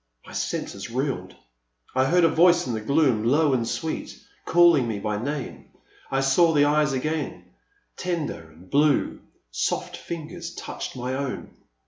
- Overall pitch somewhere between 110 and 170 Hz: Yes, medium, 140 Hz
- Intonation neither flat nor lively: Yes, average, 4.6 semitones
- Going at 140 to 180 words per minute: Yes, average, 150 wpm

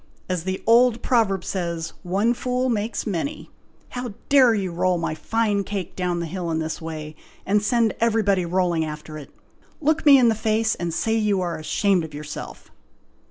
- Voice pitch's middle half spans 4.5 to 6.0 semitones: Yes, average, 5.0 semitones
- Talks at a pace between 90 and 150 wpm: No, average, 180 wpm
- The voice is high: Yes, high, 195 Hz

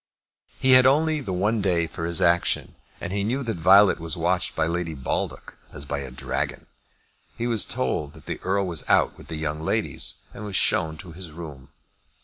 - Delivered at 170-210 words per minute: Yes, average, 200 wpm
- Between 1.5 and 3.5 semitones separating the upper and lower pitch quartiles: No, average, 4.5 semitones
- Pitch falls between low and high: No, very low, 85 Hz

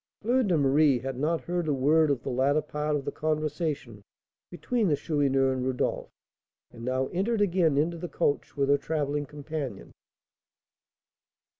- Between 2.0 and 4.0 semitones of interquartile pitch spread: Yes, average, 3.2 semitones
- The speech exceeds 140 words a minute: Yes, average, 160 wpm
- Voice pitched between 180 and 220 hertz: No, medium, 150 Hz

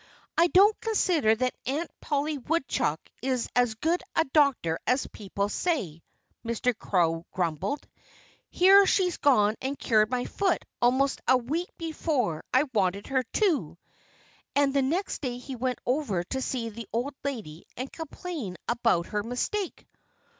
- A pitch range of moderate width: No, wide, 6.1 semitones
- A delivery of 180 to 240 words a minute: No, average, 145 wpm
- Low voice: No, very high, 255 Hz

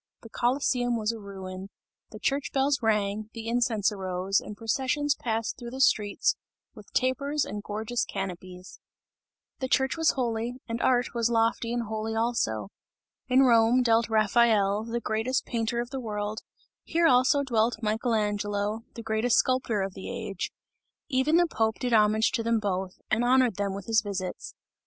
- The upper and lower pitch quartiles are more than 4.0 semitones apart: No, average, 3.0 semitones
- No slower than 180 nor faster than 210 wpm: No, average, 165 wpm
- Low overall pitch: No, high, 225 Hz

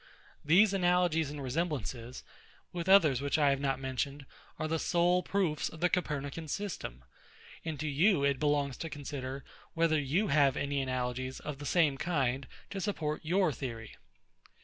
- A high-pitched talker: No, medium, 150 Hz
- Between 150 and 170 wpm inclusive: Yes, average, 160 wpm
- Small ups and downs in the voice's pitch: No, average, 4.0 semitones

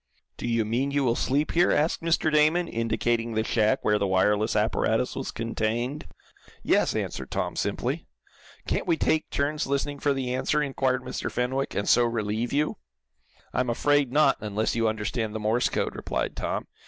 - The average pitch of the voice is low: Yes, low, 125 Hz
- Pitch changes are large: No, average, 4.5 semitones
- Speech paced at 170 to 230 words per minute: Yes, average, 175 wpm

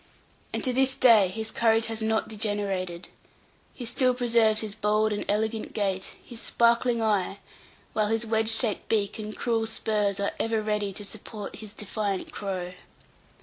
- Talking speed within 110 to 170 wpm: Yes, average, 160 wpm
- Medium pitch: No, high, 215 Hz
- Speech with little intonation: Yes, narrow, 1.7 semitones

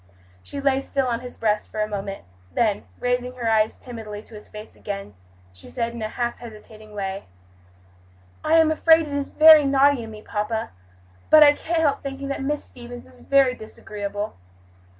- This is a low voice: No, high, 240 Hz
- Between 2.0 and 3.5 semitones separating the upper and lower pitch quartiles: No, average, 4.6 semitones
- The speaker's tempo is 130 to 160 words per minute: No, average, 185 wpm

